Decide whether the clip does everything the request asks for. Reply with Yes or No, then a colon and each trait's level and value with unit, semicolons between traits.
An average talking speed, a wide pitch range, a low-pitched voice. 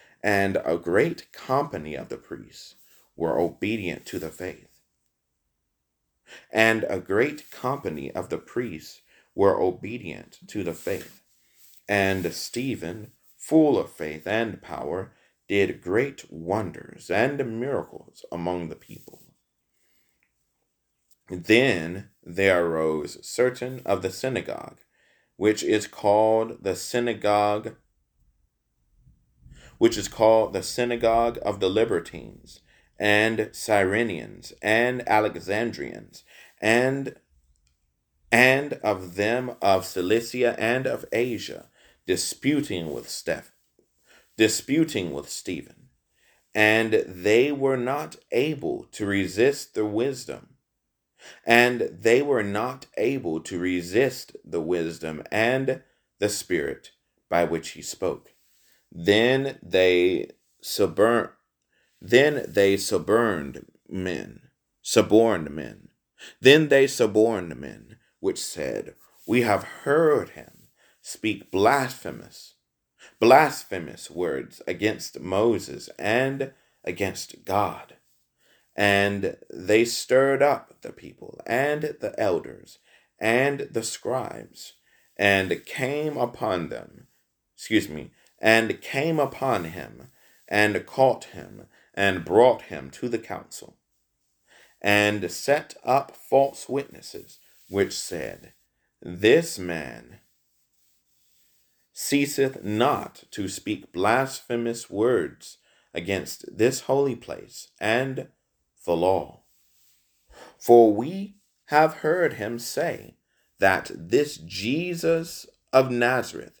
No: slow, 100 wpm; wide, 6.0 semitones; low, 110 Hz